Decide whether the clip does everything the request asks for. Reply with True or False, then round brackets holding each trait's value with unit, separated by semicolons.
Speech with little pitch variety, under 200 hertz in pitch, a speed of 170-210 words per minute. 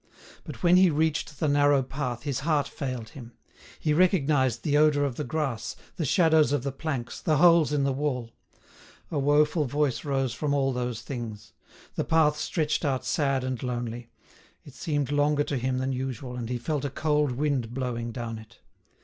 False (3.3 semitones; 140 Hz; 185 wpm)